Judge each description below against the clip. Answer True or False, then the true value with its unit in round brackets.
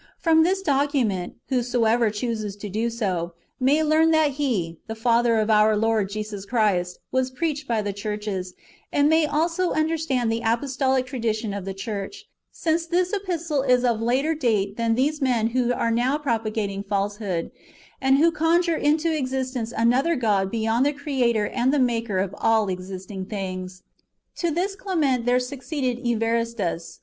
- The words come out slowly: False (160 wpm)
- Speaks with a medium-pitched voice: False (240 Hz)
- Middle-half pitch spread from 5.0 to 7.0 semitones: True (5.4 semitones)